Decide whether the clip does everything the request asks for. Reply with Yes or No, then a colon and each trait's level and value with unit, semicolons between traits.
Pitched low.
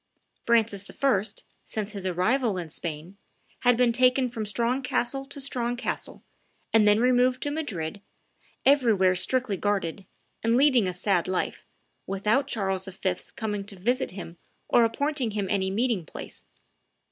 No: high, 220 Hz